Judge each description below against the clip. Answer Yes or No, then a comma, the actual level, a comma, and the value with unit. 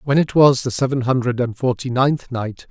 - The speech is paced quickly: Yes, fast, 220 wpm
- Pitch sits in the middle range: No, low, 130 Hz